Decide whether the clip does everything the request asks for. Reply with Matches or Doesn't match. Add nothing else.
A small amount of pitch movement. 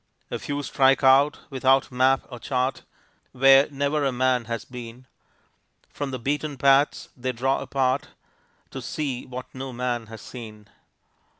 Matches